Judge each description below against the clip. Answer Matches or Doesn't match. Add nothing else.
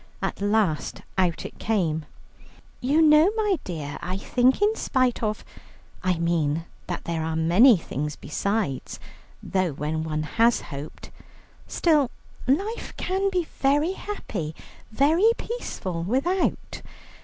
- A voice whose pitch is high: Matches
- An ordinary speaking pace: Doesn't match